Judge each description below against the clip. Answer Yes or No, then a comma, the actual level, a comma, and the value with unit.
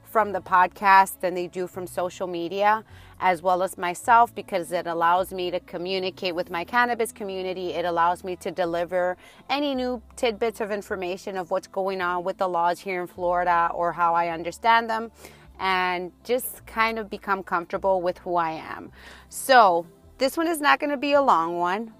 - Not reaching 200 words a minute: Yes, average, 185 wpm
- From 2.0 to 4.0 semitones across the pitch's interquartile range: Yes, average, 3.1 semitones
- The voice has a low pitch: No, medium, 185 Hz